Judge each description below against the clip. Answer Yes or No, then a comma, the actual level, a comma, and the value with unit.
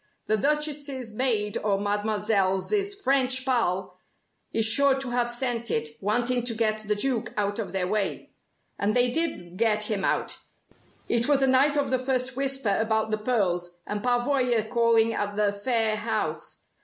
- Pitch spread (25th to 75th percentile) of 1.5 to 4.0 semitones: Yes, average, 3.7 semitones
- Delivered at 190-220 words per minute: No, average, 165 wpm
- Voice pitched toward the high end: Yes, high, 225 Hz